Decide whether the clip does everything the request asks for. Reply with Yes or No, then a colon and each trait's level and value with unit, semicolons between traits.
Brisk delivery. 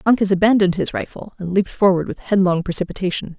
No: average, 175 wpm